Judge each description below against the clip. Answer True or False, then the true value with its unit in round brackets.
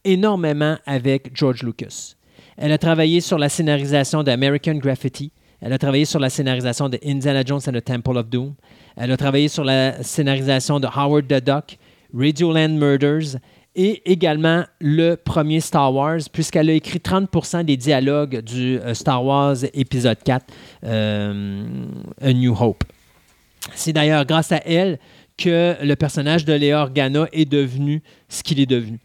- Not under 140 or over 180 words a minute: True (160 wpm)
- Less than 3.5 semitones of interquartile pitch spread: True (3.1 semitones)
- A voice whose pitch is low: False (145 Hz)